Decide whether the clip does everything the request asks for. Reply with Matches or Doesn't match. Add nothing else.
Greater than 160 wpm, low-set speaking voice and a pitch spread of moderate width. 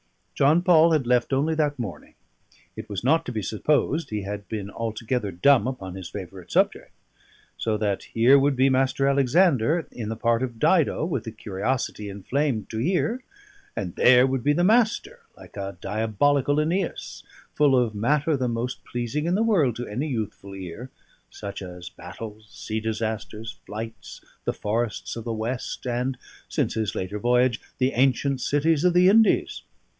Matches